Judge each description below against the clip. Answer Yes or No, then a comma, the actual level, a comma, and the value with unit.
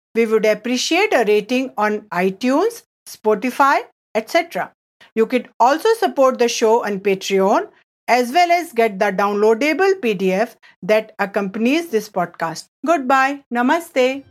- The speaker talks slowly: Yes, slow, 125 wpm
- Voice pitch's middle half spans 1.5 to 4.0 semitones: No, average, 4.6 semitones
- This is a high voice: Yes, high, 230 Hz